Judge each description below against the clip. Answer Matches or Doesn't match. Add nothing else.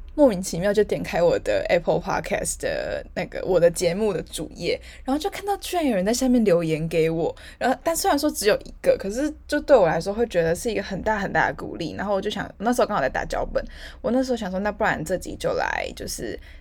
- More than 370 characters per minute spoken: Matches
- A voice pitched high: Matches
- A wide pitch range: Matches